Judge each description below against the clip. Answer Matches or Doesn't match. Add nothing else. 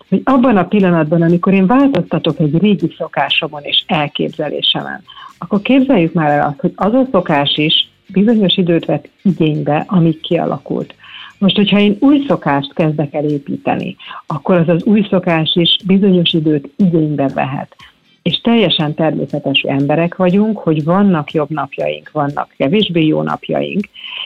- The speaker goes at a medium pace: Matches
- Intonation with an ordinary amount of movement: Matches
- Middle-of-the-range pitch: Matches